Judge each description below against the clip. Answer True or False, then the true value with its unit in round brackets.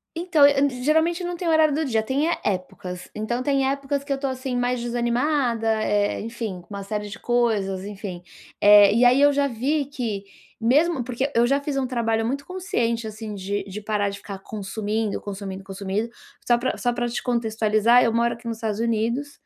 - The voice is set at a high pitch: True (235 Hz)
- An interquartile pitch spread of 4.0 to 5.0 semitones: True (4.6 semitones)